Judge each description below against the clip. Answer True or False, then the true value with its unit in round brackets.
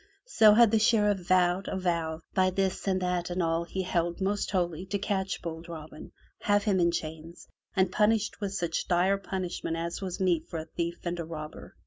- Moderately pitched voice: True (180 Hz)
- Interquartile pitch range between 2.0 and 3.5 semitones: True (2.5 semitones)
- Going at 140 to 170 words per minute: False (200 wpm)